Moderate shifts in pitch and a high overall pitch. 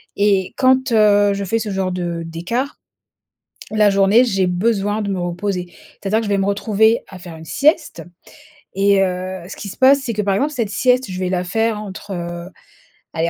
Yes: average, 3.2 semitones; high, 200 Hz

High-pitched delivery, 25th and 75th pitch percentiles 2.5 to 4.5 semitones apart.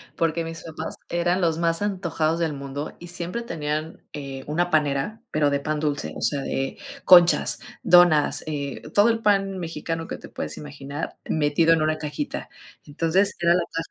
No: medium, 165 Hz; average, 2.8 semitones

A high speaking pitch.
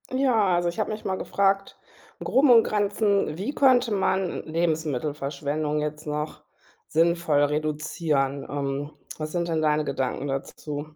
No: medium, 155 Hz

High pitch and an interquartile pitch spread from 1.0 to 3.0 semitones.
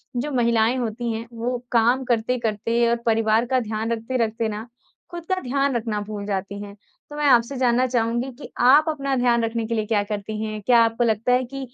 Yes: high, 235 Hz; narrow, 2.4 semitones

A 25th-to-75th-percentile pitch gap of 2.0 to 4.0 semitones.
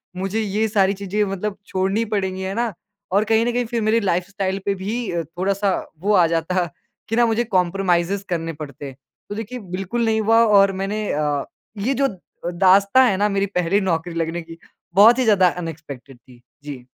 Yes: average, 3.7 semitones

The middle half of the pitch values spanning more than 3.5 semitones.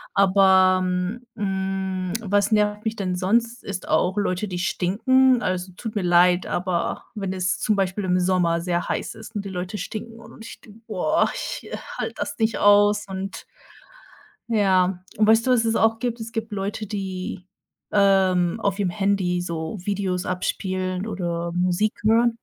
No: average, 2.7 semitones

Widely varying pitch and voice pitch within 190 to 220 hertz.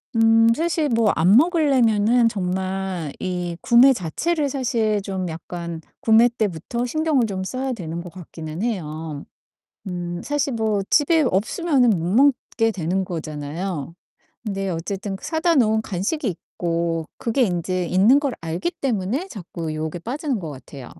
Yes: wide, 6.2 semitones; high, 200 Hz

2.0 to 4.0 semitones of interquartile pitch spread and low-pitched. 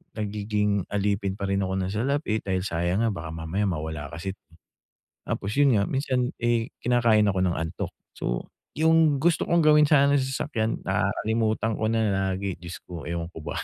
No: average, 4.7 semitones; low, 105 Hz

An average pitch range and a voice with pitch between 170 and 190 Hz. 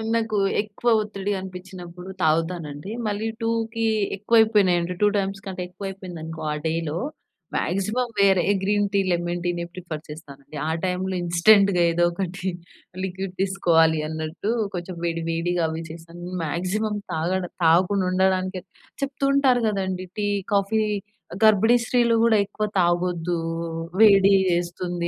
Yes: average, 3.0 semitones; medium, 185 Hz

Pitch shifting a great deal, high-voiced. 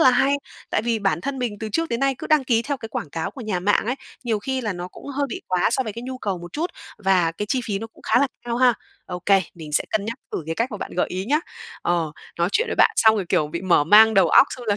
Yes: wide, 5.8 semitones; high, 220 Hz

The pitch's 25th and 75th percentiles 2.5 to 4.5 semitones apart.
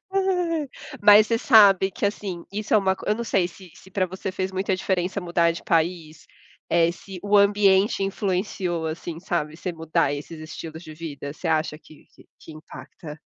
Yes: average, 3.6 semitones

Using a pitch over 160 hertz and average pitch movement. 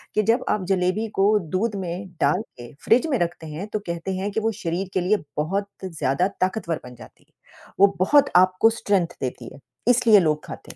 Yes: medium, 185 Hz; average, 3.9 semitones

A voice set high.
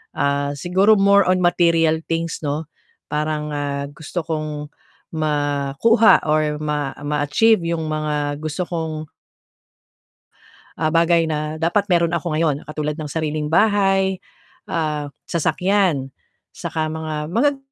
No: medium, 155 Hz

